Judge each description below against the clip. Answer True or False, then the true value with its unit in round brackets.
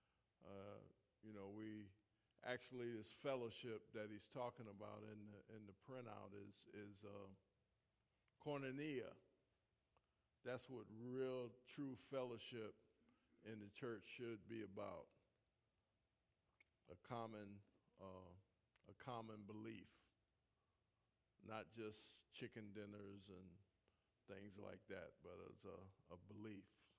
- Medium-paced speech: False (110 wpm)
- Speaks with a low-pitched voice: True (110 Hz)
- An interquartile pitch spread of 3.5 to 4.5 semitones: False (2.4 semitones)